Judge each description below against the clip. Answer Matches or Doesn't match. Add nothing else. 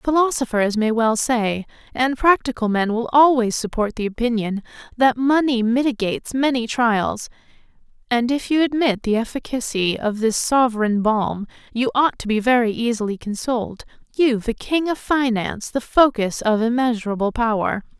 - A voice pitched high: Matches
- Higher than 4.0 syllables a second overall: Matches